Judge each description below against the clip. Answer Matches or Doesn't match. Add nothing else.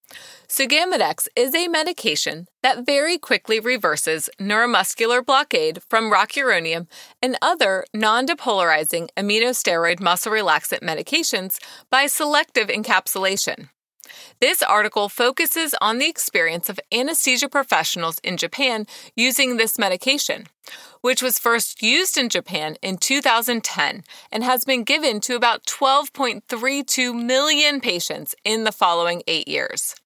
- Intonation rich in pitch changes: Matches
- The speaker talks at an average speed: Doesn't match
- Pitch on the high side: Matches